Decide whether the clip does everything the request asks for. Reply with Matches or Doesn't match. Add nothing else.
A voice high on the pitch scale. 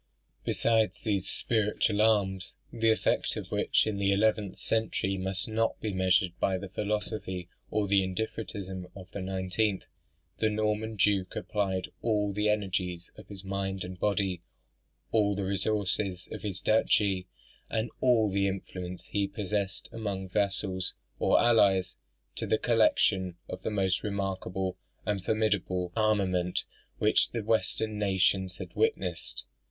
Doesn't match